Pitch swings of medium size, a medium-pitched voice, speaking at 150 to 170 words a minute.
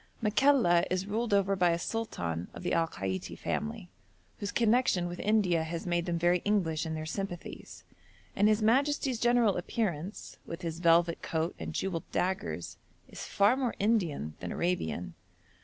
Yes: average, 4.5 semitones; medium, 180 Hz; average, 160 wpm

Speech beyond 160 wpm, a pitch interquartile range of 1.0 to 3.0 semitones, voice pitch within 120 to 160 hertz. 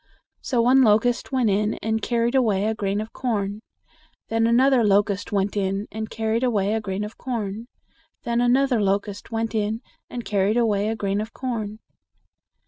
No: average, 170 wpm; narrow, 2.5 semitones; high, 220 Hz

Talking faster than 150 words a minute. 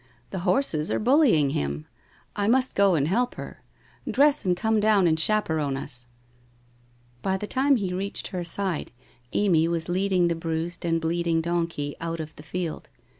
Yes: average, 175 wpm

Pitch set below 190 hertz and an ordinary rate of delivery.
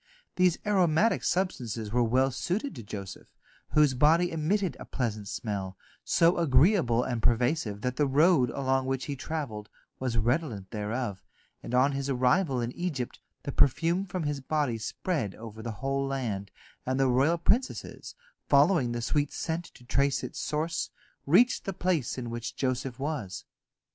Yes: low, 135 Hz; average, 160 wpm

